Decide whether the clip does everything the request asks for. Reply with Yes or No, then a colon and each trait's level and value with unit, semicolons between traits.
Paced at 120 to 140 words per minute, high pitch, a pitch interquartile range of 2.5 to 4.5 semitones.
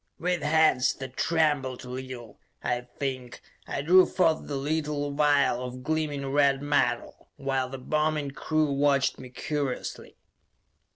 No: slow, 135 wpm; medium, 140 Hz; average, 2.8 semitones